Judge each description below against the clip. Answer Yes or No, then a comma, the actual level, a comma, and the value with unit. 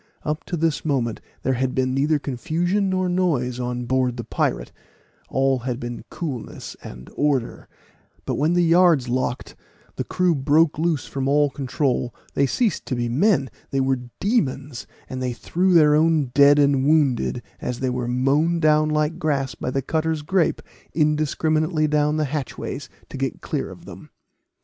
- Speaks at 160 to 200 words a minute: Yes, average, 170 wpm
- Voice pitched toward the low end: No, medium, 145 Hz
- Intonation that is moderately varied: Yes, average, 3.6 semitones